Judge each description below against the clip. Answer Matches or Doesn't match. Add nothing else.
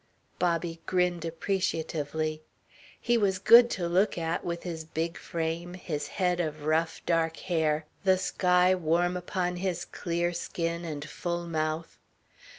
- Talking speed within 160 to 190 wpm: Doesn't match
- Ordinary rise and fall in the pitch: Doesn't match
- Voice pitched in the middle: Matches